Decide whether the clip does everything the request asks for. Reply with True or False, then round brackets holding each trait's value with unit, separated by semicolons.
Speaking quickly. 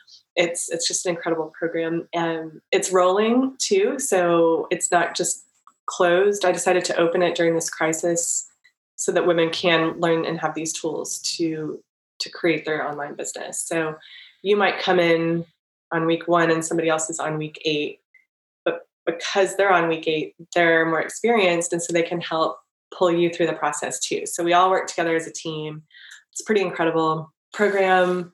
False (180 wpm)